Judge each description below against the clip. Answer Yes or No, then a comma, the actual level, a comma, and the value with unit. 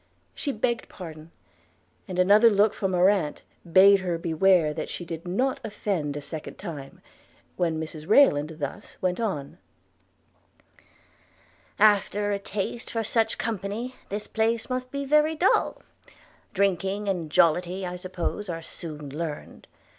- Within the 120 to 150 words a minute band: Yes, average, 140 wpm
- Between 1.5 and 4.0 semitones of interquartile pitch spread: No, average, 4.5 semitones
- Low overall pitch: No, high, 190 Hz